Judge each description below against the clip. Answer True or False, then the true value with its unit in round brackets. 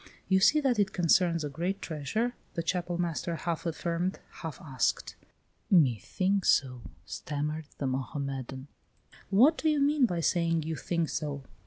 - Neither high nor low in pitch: True (170 Hz)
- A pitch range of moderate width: True (4.3 semitones)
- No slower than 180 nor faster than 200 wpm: False (155 wpm)